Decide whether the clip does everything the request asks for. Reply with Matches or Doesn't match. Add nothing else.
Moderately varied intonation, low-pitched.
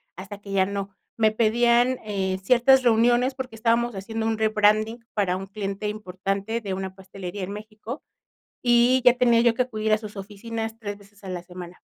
Doesn't match